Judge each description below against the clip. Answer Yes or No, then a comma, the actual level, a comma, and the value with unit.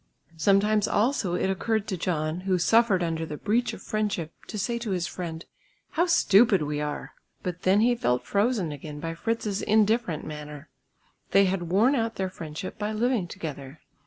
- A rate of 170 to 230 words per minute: Yes, average, 175 wpm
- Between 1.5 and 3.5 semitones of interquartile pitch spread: No, average, 5.1 semitones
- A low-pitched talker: No, high, 190 Hz